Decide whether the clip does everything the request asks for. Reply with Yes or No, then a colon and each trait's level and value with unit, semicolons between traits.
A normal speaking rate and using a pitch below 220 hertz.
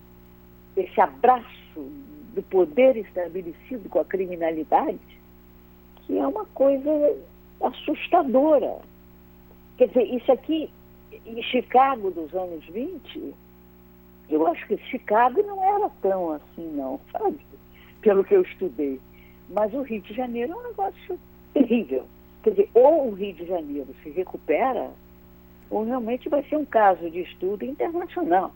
Yes: average, 130 wpm; high, 190 Hz